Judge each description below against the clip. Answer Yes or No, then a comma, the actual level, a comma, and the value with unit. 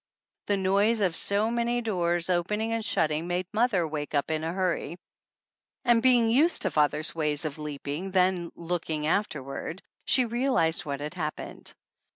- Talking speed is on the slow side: No, average, 175 wpm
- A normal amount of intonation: No, wide, 5.9 semitones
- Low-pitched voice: No, medium, 180 Hz